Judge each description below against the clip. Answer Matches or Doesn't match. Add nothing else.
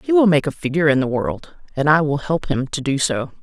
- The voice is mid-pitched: Matches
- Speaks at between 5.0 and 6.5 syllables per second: Matches